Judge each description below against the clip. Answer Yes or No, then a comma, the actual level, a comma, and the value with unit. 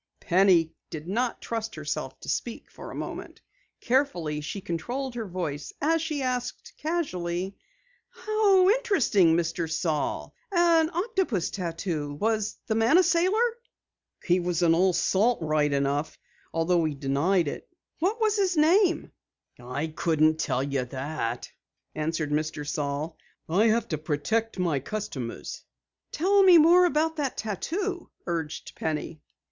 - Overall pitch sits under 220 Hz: Yes, medium, 185 Hz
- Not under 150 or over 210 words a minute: No, average, 140 wpm